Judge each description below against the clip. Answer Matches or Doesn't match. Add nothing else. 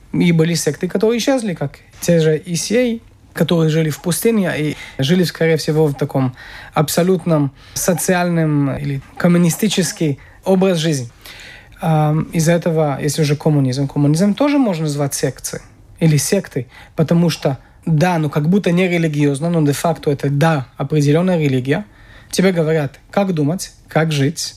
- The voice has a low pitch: Doesn't match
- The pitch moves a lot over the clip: Doesn't match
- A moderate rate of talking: Matches